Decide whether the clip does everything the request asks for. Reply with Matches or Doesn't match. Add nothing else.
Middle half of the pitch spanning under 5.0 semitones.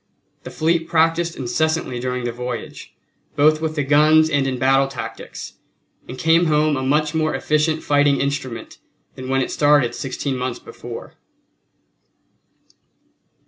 Matches